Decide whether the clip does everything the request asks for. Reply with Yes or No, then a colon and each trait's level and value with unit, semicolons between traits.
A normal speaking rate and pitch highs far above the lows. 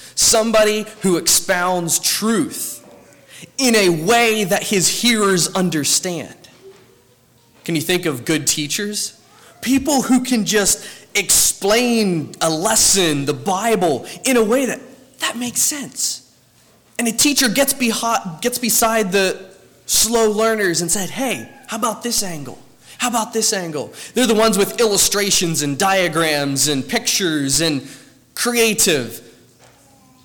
No: slow, 130 wpm; wide, 5.8 semitones